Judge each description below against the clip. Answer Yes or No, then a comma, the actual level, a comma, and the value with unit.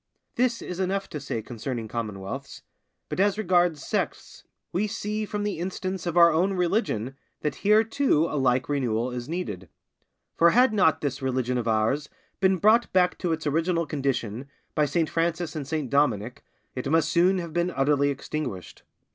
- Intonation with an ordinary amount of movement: No, wide, 6.0 semitones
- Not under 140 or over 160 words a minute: No, average, 170 wpm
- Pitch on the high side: No, medium, 160 Hz